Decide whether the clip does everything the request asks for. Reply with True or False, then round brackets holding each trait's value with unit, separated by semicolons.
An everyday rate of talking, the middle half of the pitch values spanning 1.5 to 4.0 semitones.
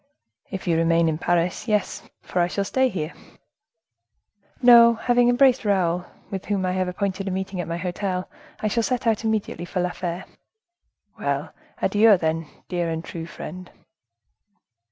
True (165 wpm; 3.6 semitones)